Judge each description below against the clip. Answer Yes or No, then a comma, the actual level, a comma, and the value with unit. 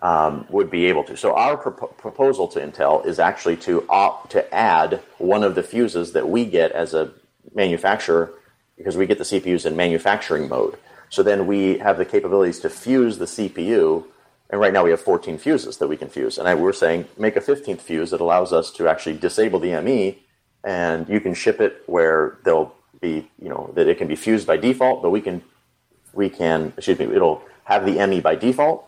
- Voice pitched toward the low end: No, medium, 160 Hz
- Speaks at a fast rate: Yes, fast, 210 wpm